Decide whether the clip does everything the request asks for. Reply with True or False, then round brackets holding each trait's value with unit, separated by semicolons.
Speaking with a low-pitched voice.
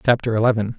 True (115 Hz)